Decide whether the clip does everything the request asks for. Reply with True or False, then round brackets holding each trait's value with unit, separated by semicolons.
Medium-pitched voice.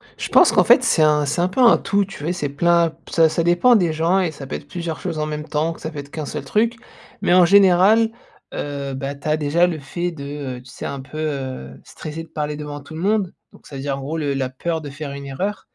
True (155 Hz)